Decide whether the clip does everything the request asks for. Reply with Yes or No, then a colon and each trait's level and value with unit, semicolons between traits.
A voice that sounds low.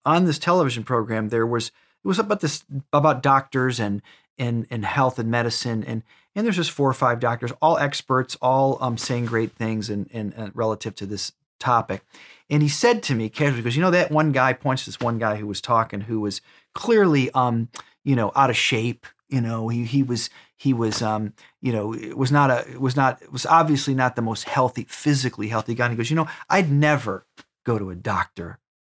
Yes: low, 125 Hz